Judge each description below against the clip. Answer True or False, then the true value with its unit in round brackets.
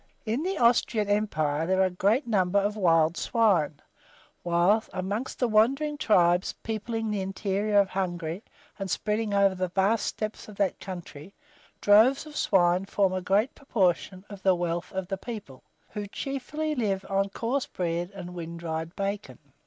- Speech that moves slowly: False (165 wpm)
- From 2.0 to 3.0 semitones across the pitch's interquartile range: False (3.4 semitones)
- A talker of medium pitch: False (195 Hz)